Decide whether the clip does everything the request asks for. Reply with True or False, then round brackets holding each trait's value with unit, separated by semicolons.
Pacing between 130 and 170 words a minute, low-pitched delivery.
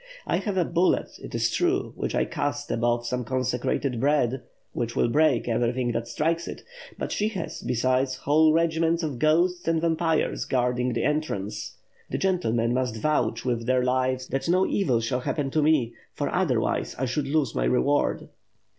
False (180 wpm; 130 Hz)